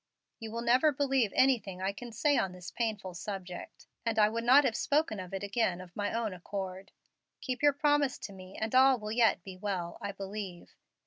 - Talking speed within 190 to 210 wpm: Yes, fast, 205 wpm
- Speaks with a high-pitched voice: Yes, high, 215 Hz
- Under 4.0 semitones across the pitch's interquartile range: No, average, 4.9 semitones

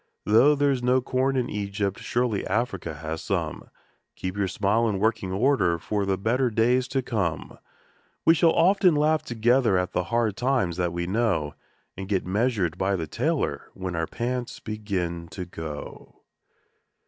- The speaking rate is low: No, average, 165 wpm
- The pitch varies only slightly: No, average, 5.3 semitones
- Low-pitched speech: Yes, low, 105 Hz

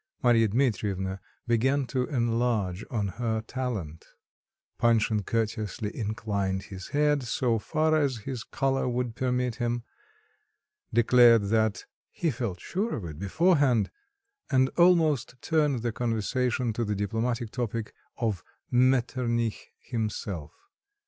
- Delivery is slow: Yes, slow, 115 wpm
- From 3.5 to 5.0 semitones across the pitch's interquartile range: No, average, 3.1 semitones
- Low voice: Yes, low, 115 Hz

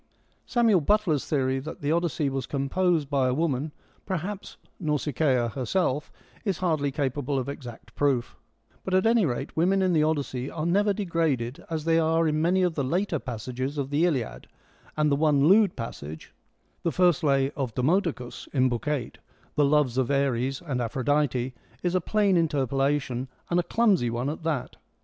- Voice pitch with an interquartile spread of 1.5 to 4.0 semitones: No, average, 4.4 semitones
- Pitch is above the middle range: No, medium, 150 Hz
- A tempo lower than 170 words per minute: No, average, 175 wpm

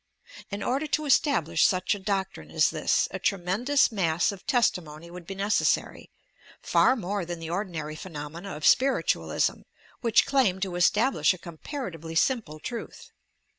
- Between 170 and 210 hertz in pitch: Yes, high, 190 Hz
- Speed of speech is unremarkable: Yes, average, 160 wpm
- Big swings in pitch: Yes, wide, 5.7 semitones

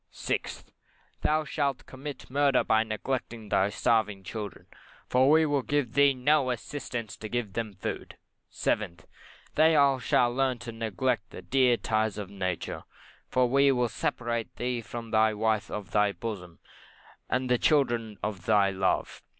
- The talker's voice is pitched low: Yes, low, 115 Hz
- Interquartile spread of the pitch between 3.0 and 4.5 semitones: Yes, average, 3.9 semitones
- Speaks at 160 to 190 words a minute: No, average, 150 wpm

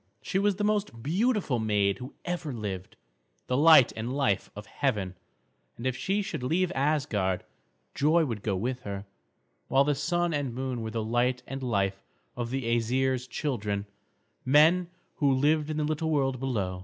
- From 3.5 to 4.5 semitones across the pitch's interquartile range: No, average, 5.3 semitones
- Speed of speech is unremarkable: Yes, average, 170 wpm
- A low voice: Yes, low, 130 Hz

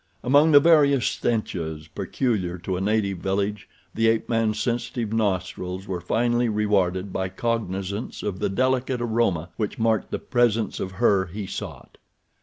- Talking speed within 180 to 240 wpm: No, average, 150 wpm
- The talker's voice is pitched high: No, low, 105 Hz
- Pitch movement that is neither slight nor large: Yes, average, 3.9 semitones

